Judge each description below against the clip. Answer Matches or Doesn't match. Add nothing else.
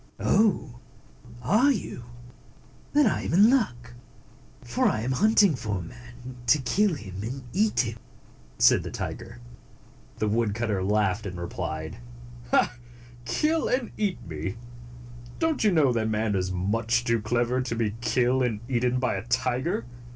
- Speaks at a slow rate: Doesn't match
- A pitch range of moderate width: Doesn't match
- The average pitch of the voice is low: Matches